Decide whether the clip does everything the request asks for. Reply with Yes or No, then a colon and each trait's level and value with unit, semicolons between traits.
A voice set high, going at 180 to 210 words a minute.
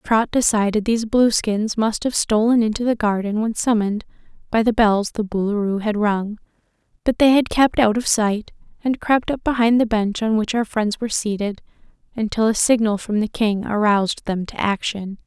Yes: high, 220 Hz; average, 190 wpm